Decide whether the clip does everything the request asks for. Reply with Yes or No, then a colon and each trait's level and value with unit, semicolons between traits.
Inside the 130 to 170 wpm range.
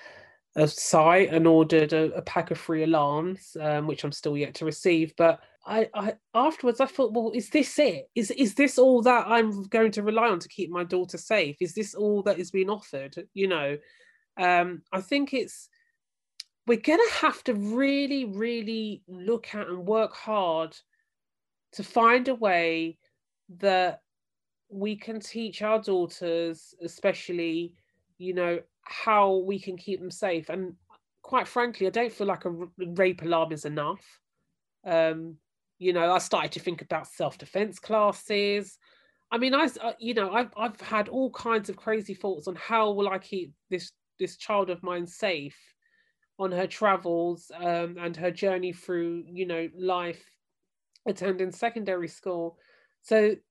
Yes: average, 165 wpm